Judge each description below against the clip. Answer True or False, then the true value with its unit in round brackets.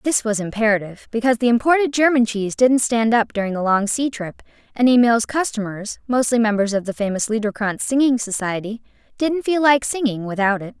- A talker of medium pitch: False (230 Hz)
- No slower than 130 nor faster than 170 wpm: False (185 wpm)